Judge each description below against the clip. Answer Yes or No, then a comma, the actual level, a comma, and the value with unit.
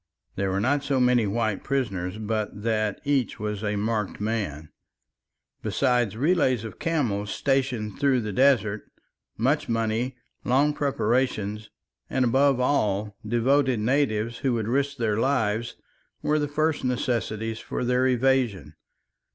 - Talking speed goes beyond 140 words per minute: No, slow, 135 wpm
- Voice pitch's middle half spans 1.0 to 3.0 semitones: No, average, 3.9 semitones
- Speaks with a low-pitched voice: Yes, low, 120 Hz